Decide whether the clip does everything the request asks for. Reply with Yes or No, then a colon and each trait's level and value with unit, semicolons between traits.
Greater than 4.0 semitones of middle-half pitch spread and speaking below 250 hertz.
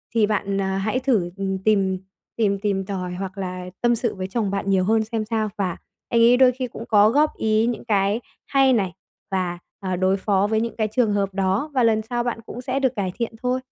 No: average, 3.3 semitones; high, 210 Hz